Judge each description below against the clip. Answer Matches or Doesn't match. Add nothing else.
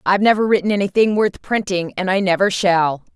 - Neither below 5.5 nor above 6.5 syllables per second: Matches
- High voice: Matches